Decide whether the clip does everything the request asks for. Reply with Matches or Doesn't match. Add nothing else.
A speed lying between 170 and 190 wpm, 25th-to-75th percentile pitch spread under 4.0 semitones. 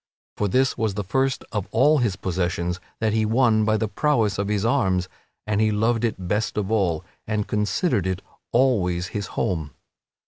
Matches